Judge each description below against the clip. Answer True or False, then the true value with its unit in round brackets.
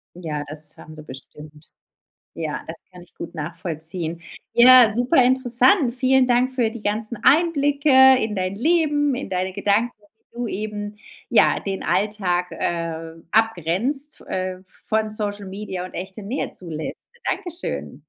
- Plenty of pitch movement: True (6.2 semitones)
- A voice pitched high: True (210 Hz)